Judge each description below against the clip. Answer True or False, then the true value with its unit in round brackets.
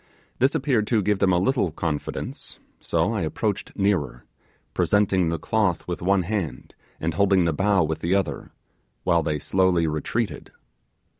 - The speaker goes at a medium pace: True (155 wpm)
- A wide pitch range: False (3.6 semitones)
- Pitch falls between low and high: False (95 Hz)